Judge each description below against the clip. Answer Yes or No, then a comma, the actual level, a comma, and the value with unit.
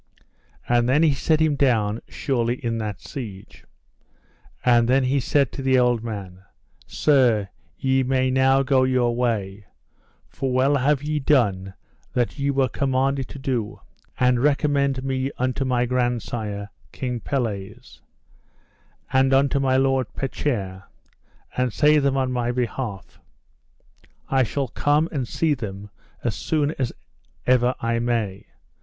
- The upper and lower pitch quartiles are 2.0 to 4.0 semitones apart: Yes, average, 2.7 semitones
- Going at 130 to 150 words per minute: Yes, average, 140 wpm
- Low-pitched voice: Yes, low, 130 Hz